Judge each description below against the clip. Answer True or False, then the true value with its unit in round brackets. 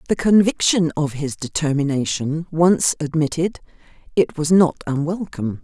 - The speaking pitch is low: False (155 Hz)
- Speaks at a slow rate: True (115 wpm)